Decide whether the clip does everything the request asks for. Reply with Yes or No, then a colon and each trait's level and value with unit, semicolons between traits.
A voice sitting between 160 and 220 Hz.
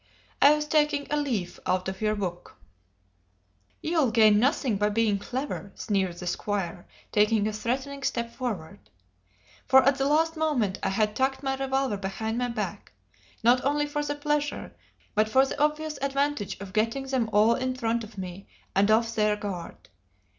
No: high, 235 Hz